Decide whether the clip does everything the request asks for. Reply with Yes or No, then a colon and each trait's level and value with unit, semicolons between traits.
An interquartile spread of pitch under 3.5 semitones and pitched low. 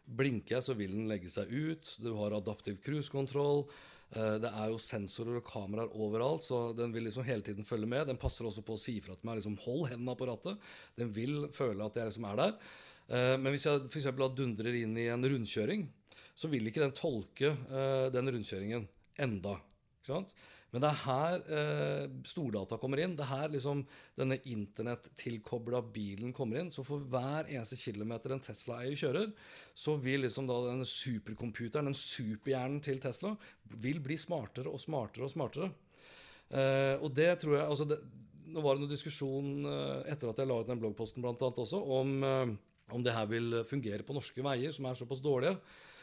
No: average, 3.8 semitones; low, 125 Hz